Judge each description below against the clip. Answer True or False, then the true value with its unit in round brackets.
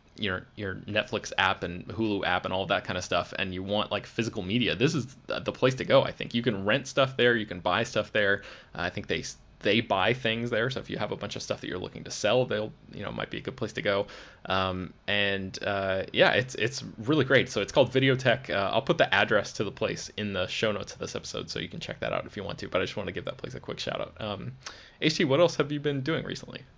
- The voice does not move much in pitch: False (4.6 semitones)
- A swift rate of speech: True (285 wpm)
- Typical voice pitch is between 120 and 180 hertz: False (110 Hz)